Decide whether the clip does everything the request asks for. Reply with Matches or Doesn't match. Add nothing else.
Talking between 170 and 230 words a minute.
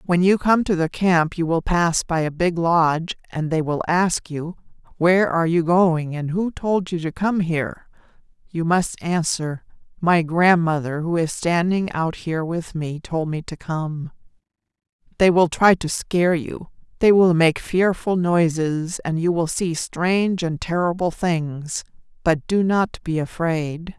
Matches